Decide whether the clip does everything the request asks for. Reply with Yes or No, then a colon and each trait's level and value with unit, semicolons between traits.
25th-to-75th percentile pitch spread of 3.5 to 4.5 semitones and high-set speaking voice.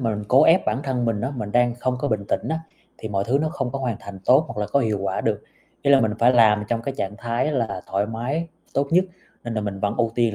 No: average, 4.2 semitones; low, 120 Hz